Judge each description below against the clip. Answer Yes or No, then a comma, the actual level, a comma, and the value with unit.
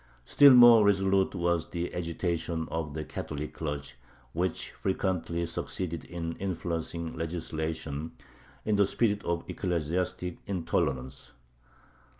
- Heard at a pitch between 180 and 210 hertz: No, very low, 85 Hz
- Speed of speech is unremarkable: No, slow, 110 wpm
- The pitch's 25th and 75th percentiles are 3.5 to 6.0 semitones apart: No, average, 2.7 semitones